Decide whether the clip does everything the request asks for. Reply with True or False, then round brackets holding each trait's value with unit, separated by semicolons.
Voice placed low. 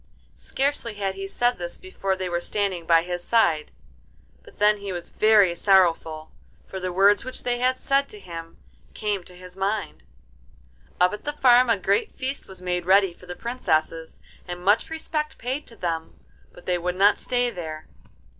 False (195 Hz)